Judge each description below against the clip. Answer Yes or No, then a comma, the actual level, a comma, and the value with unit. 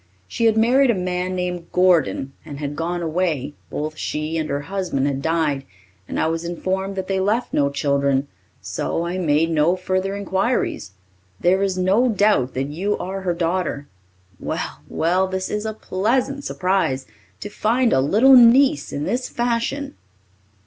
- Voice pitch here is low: No, medium, 180 Hz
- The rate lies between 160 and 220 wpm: Yes, average, 165 wpm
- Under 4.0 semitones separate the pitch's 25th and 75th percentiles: No, average, 5.0 semitones